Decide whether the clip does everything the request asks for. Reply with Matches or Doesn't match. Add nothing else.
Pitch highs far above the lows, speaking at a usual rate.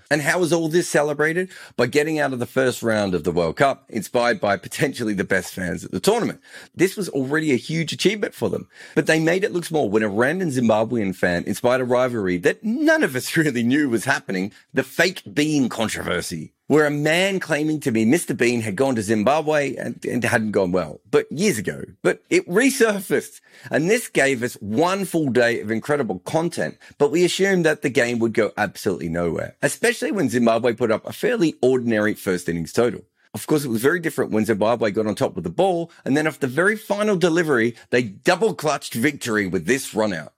Doesn't match